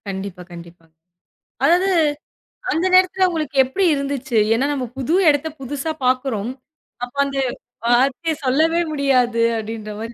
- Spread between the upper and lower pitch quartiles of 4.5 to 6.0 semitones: Yes, average, 5.0 semitones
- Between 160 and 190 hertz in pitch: No, very high, 265 Hz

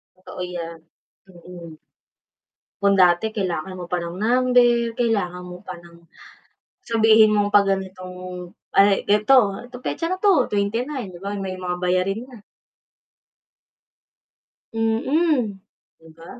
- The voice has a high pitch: Yes, high, 200 Hz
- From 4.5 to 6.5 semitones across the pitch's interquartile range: No, average, 4.1 semitones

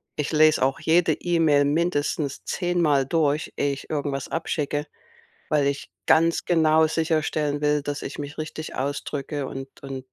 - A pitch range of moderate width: No, narrow, 2.0 semitones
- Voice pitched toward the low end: No, medium, 150 Hz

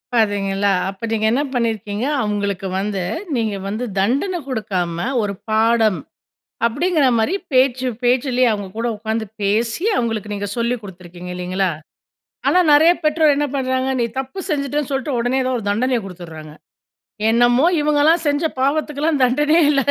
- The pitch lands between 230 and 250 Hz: Yes, high, 235 Hz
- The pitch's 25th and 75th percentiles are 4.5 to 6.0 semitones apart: Yes, wide, 5.4 semitones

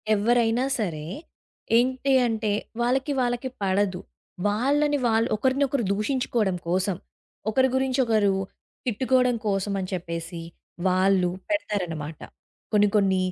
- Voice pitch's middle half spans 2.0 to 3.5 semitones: No, average, 5.2 semitones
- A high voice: Yes, high, 215 Hz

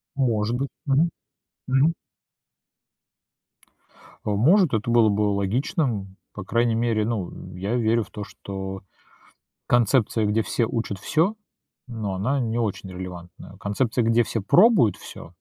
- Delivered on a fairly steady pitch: No, average, 3.6 semitones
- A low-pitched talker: Yes, low, 115 Hz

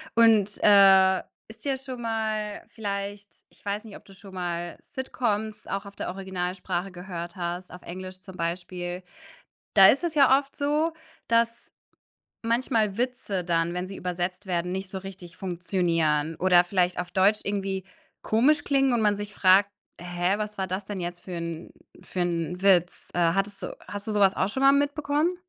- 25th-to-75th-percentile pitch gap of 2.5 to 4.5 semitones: Yes, average, 3.4 semitones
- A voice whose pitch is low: No, high, 195 Hz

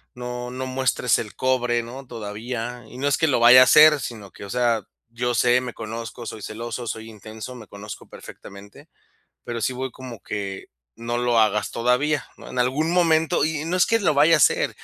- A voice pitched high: No, low, 120 Hz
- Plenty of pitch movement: No, narrow, 2.6 semitones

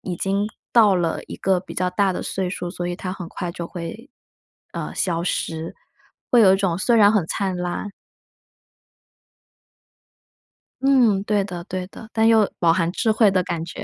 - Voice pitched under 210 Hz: Yes, high, 190 Hz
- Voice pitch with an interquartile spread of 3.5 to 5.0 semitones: No, average, 2.9 semitones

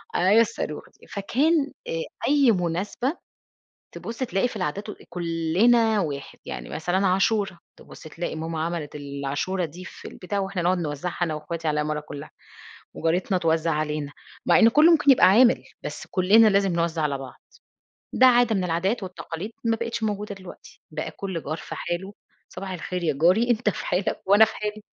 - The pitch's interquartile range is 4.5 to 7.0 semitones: Yes, average, 5.0 semitones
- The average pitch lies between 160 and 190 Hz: Yes, medium, 185 Hz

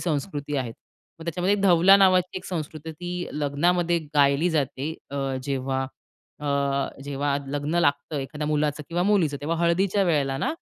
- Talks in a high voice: No, medium, 150 Hz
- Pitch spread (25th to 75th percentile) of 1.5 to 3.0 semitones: No, average, 3.6 semitones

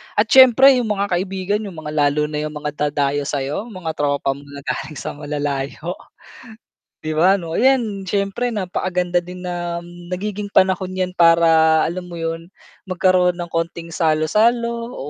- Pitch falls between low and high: Yes, medium, 175 Hz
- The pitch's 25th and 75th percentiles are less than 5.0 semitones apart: Yes, average, 3.7 semitones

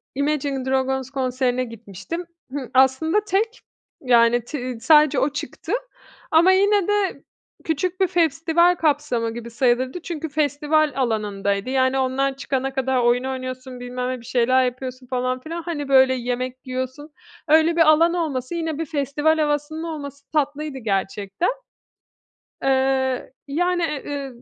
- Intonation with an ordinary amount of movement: Yes, average, 3.6 semitones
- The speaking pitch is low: No, very high, 270 Hz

